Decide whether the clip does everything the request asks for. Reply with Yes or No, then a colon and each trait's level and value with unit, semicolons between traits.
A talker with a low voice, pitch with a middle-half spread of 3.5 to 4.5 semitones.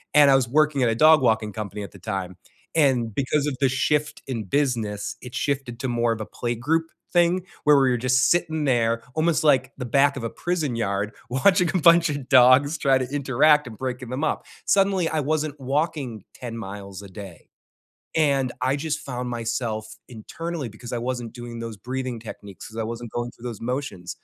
Yes: low, 130 Hz; average, 4.1 semitones